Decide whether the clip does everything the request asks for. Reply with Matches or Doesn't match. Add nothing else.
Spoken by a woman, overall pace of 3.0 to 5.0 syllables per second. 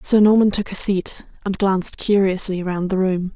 Matches